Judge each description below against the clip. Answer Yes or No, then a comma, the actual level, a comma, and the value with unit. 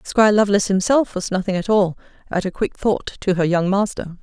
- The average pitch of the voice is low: No, high, 195 Hz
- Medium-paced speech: No, fast, 215 wpm